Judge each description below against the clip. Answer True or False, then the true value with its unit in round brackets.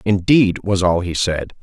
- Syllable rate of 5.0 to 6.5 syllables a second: False (4.1 syllables/s)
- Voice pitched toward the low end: True (95 Hz)